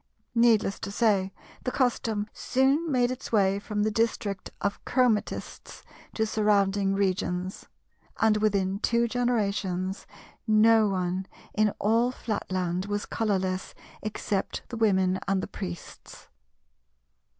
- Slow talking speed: Yes, slow, 115 wpm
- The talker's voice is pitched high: Yes, high, 210 Hz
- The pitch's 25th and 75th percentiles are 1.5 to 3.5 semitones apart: Yes, average, 2.9 semitones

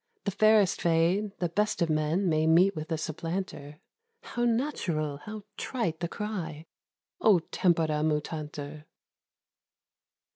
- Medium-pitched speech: Yes, medium, 165 Hz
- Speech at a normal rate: No, slow, 120 wpm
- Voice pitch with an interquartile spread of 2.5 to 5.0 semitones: Yes, average, 4.6 semitones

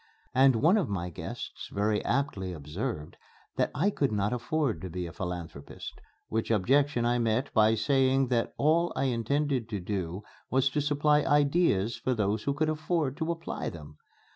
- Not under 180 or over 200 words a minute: No, average, 170 wpm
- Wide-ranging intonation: Yes, wide, 6.1 semitones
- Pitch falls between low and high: No, low, 125 Hz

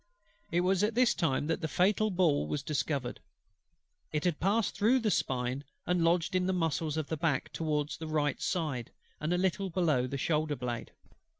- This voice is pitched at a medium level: Yes, medium, 160 Hz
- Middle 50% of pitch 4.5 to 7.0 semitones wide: No, average, 3.9 semitones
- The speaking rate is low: No, average, 190 wpm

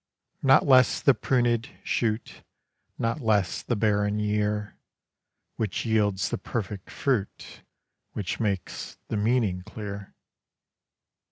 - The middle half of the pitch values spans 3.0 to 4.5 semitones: No, narrow, 2.4 semitones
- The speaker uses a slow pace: Yes, slow, 105 wpm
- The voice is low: Yes, low, 105 Hz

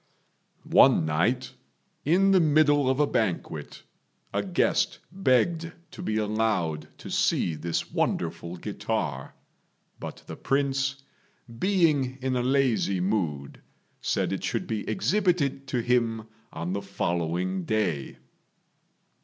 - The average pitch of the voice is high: No, low, 120 Hz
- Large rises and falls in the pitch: Yes, wide, 7.5 semitones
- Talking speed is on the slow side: Yes, slow, 120 wpm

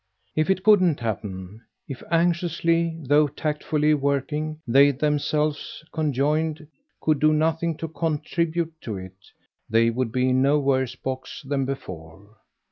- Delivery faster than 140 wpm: No, slow, 135 wpm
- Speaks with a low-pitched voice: No, medium, 145 Hz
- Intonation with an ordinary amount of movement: Yes, average, 3.6 semitones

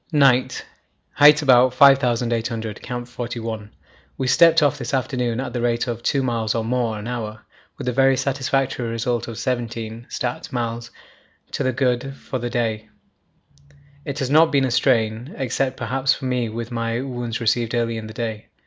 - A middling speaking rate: Yes, average, 175 wpm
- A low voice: Yes, low, 120 Hz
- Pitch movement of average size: No, narrow, 2.3 semitones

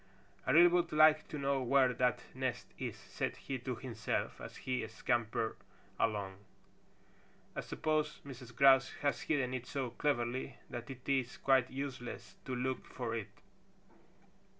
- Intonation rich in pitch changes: No, narrow, 2.4 semitones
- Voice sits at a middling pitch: No, low, 130 Hz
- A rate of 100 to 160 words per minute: Yes, average, 150 wpm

